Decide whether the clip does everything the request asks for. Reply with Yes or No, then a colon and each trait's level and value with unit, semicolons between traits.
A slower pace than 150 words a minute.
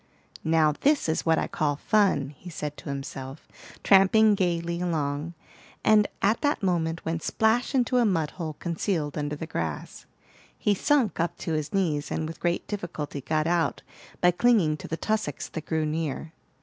No: average, 175 wpm